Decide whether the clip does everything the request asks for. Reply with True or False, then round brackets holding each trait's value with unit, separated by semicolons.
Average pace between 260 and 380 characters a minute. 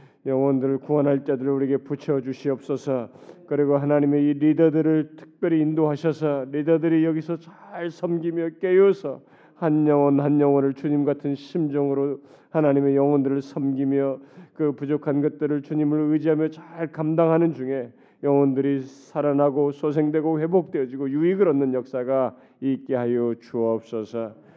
True (330 characters per minute)